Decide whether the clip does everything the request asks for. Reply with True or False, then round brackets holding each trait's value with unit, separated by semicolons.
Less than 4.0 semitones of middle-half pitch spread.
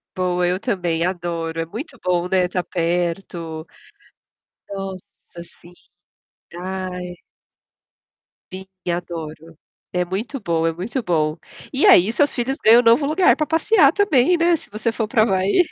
False (5.5 semitones)